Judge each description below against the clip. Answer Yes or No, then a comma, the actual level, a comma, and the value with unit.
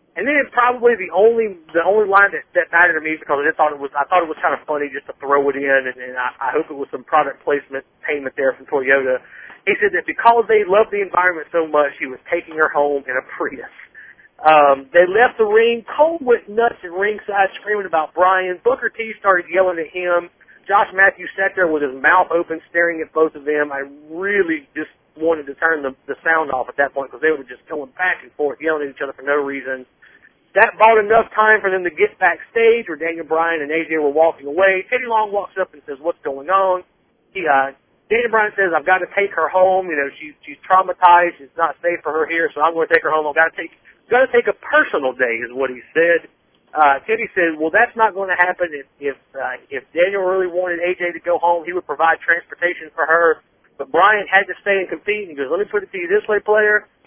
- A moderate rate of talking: No, fast, 250 wpm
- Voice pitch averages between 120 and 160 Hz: No, medium, 170 Hz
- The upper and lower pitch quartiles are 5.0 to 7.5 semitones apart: Yes, average, 5.3 semitones